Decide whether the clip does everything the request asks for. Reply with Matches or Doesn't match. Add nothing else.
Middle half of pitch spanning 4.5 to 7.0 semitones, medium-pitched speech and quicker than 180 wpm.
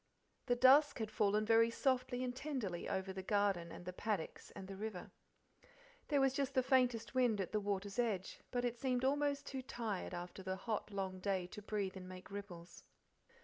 Doesn't match